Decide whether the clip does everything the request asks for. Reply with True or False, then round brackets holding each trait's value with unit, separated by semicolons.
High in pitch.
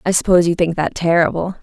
False (170 Hz)